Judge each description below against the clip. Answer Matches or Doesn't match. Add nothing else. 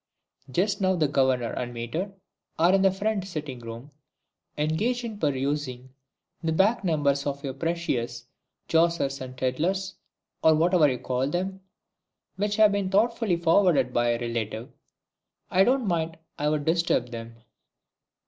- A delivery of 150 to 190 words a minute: Doesn't match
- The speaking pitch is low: Doesn't match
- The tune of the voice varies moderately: Doesn't match